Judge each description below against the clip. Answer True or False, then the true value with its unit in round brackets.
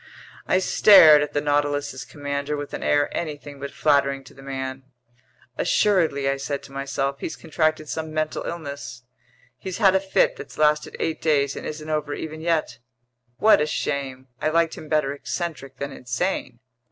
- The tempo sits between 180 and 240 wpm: False (170 wpm)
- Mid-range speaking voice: True (145 Hz)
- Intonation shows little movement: True (2.3 semitones)